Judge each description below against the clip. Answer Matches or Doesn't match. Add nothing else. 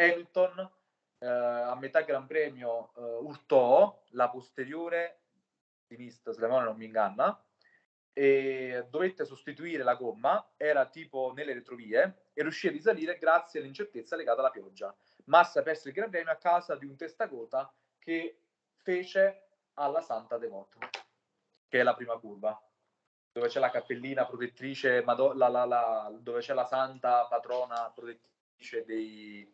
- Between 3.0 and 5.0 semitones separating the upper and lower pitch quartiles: Doesn't match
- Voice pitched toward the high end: Doesn't match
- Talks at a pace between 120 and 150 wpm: Matches